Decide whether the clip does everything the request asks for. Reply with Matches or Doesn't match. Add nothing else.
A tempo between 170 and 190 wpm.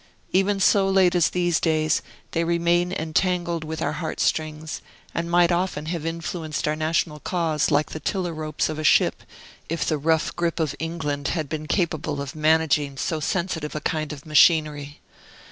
Matches